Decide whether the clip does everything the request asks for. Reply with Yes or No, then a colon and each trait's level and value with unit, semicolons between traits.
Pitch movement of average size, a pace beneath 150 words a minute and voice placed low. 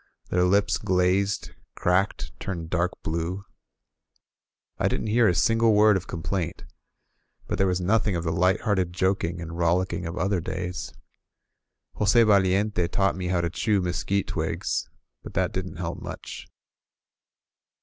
No: narrow, 2.3 semitones; average, 140 wpm; very low, 90 Hz